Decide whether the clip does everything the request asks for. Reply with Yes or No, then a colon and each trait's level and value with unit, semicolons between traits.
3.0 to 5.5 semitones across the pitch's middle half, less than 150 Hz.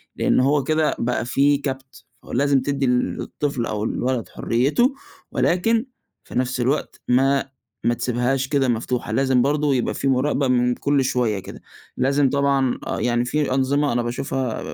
No: narrow, 2.4 semitones; low, 135 Hz